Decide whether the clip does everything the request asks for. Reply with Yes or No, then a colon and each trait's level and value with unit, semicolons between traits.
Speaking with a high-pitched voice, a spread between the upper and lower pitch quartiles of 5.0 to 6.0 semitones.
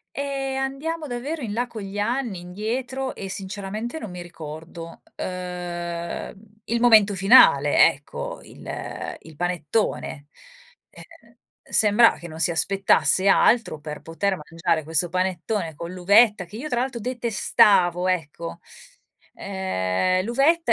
Yes: high, 195 Hz; wide, 5.5 semitones